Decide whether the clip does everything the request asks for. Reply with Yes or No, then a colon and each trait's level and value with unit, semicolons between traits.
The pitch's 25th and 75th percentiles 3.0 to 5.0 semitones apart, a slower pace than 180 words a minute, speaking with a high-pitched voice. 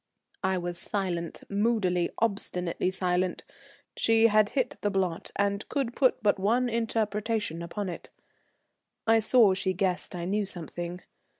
Yes: average, 3.7 semitones; slow, 135 wpm; high, 200 Hz